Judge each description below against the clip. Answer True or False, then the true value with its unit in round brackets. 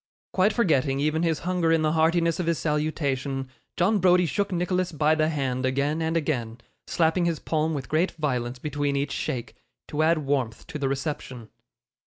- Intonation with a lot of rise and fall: False (3.4 semitones)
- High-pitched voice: False (155 Hz)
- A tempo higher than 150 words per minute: True (180 wpm)